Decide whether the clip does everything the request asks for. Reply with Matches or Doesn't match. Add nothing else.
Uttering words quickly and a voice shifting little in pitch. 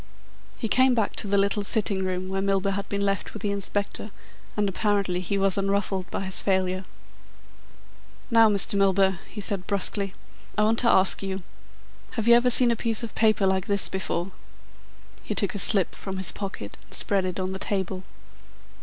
Doesn't match